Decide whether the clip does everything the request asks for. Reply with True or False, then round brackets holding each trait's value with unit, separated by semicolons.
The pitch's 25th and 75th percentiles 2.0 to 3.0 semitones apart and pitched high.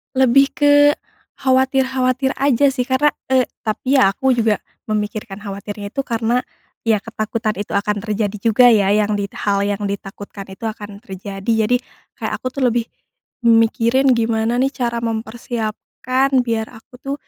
False (3.6 semitones; 230 Hz)